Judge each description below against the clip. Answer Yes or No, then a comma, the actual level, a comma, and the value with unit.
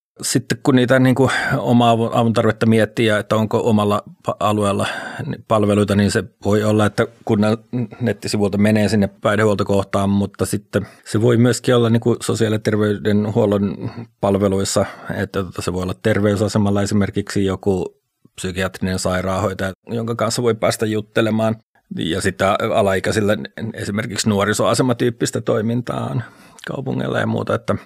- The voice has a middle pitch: No, low, 105 Hz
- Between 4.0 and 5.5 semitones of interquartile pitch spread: No, narrow, 2.4 semitones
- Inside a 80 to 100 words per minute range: No, average, 125 wpm